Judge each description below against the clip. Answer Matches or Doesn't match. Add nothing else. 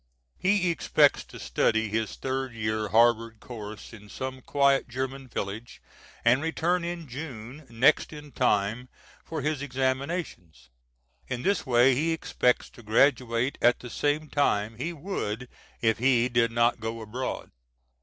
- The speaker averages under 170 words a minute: Matches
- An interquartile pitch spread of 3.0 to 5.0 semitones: Matches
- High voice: Doesn't match